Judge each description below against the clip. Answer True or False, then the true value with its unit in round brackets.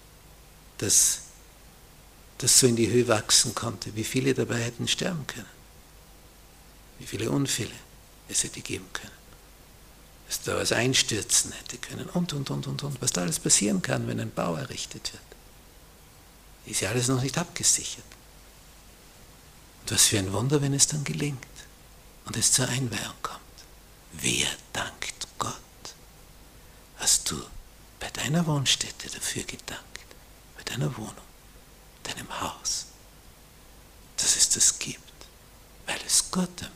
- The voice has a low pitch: True (120 Hz)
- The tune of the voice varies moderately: False (6.1 semitones)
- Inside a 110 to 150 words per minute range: True (135 wpm)